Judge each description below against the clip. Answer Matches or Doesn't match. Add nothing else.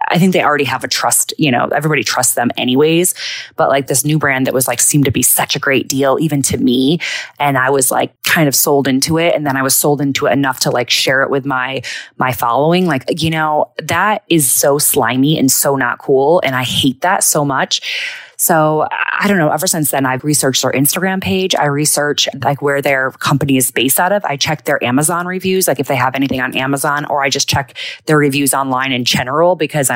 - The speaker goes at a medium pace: Doesn't match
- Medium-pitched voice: Matches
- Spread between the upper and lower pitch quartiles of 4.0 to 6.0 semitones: Doesn't match